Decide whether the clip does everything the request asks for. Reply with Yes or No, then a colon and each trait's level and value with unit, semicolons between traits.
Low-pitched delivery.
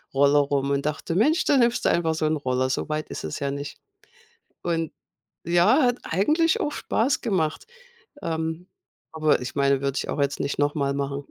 No: medium, 155 Hz